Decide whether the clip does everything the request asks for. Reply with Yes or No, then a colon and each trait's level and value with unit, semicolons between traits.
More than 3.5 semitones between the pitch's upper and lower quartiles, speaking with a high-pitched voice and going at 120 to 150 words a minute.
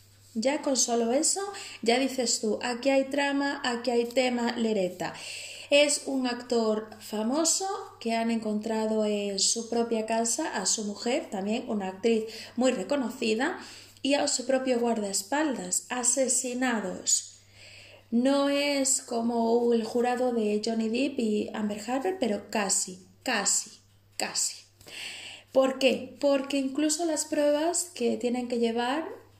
Yes: average, 4.1 semitones; high, 240 Hz; average, 130 wpm